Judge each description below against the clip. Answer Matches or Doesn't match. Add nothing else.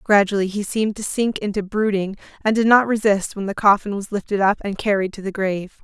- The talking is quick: Matches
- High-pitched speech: Matches